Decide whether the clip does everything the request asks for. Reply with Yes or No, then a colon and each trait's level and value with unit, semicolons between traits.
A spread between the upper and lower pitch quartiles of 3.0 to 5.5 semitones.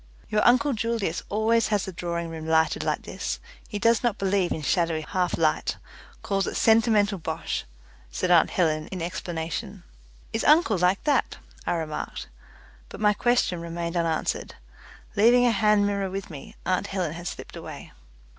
Yes: average, 4.2 semitones